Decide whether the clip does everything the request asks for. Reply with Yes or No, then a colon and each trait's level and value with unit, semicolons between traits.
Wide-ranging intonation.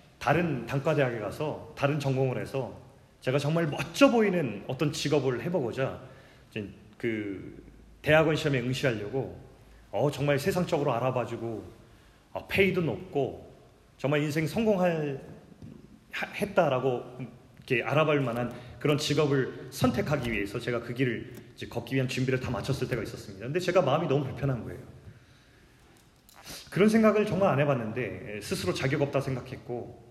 No: average, 3.7 semitones